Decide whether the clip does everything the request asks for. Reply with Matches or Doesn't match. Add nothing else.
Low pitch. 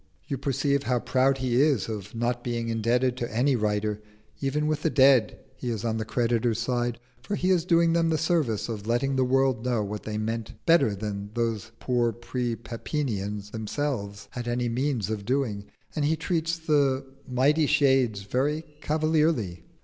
Matches